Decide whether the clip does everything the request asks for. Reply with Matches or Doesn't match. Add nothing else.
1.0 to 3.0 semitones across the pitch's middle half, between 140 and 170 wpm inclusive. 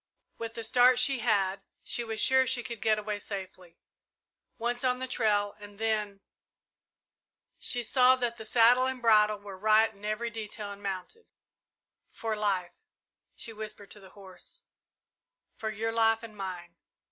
Matches